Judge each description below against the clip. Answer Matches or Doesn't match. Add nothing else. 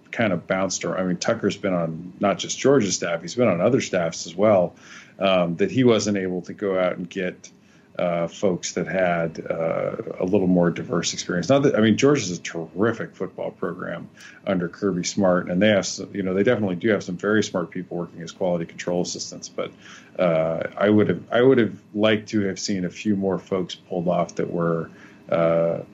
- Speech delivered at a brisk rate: Matches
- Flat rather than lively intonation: Doesn't match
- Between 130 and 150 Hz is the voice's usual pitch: Doesn't match